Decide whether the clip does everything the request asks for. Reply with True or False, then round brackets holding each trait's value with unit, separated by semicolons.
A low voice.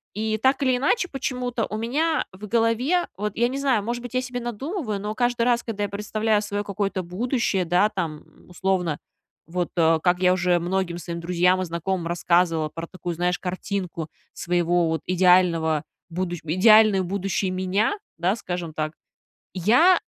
False (190 Hz)